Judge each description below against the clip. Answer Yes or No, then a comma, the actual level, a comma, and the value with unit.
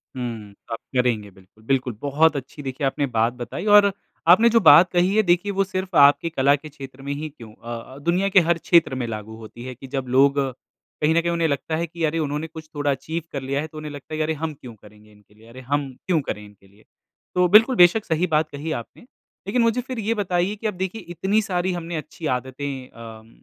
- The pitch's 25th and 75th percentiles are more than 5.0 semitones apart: Yes, wide, 5.4 semitones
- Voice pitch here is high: No, medium, 150 Hz